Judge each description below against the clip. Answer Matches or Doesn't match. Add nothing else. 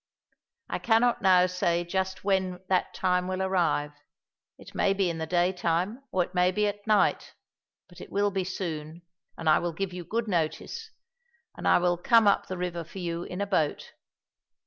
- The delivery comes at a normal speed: Matches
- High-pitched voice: Doesn't match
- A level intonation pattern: Matches